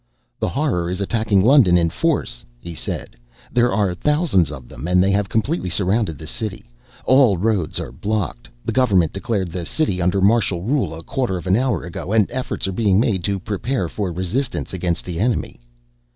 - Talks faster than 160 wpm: Yes, average, 190 wpm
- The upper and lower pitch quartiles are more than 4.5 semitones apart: Yes, average, 5.0 semitones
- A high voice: No, very low, 95 Hz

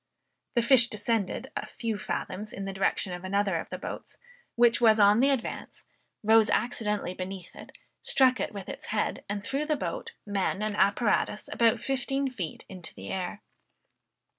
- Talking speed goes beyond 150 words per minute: Yes, average, 170 wpm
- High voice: Yes, high, 210 Hz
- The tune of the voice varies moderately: Yes, average, 3.4 semitones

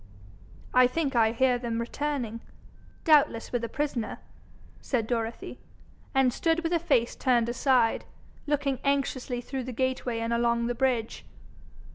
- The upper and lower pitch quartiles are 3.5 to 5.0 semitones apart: No, average, 2.9 semitones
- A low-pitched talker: No, very high, 250 Hz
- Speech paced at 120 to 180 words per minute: Yes, average, 140 wpm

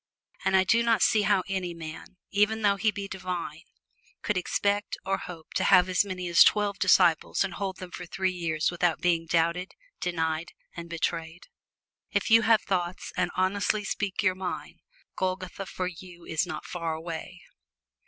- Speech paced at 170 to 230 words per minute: Yes, average, 175 wpm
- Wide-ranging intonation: No, average, 2.7 semitones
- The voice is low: No, medium, 185 Hz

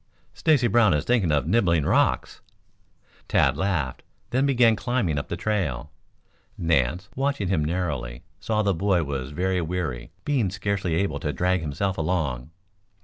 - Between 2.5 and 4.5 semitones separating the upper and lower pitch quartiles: No, wide, 5.4 semitones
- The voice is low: Yes, very low, 90 Hz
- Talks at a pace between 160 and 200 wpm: No, average, 150 wpm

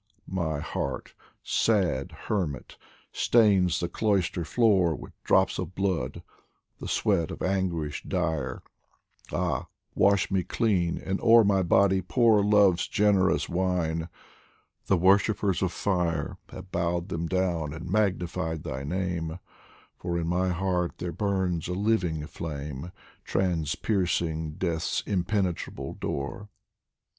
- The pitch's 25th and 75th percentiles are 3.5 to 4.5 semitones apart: No, average, 2.9 semitones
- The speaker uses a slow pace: Yes, slow, 120 wpm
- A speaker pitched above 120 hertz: No, very low, 90 Hz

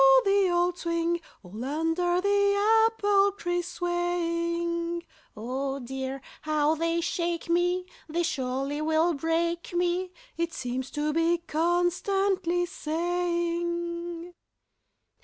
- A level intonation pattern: Yes, narrow, 1.8 semitones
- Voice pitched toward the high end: Yes, very high, 340 Hz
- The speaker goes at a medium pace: No, slow, 100 wpm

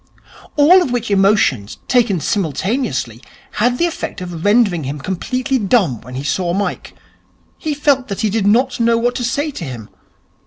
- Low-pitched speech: No, high, 210 Hz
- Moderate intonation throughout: No, wide, 6.9 semitones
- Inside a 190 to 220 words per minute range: No, average, 170 wpm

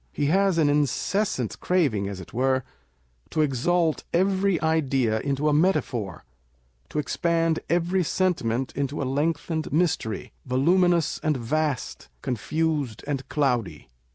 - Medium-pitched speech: Yes, medium, 150 Hz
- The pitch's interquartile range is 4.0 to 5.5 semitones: Yes, average, 4.6 semitones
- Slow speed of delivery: Yes, slow, 125 wpm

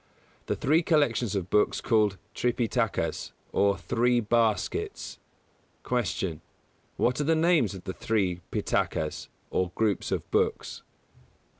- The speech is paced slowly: Yes, slow, 125 wpm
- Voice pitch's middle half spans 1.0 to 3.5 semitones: No, average, 4.2 semitones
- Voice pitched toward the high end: No, low, 110 Hz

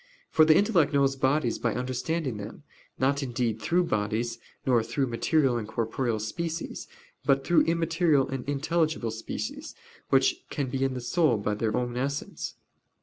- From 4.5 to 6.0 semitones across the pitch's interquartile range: Yes, average, 5.2 semitones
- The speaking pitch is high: No, low, 135 Hz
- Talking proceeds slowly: No, average, 155 wpm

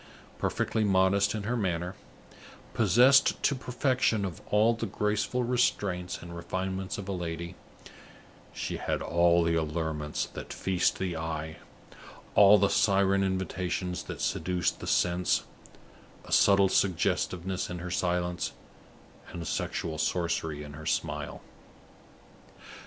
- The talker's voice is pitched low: Yes, very low, 90 Hz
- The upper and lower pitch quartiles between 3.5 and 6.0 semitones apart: No, average, 2.8 semitones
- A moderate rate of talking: No, slow, 125 wpm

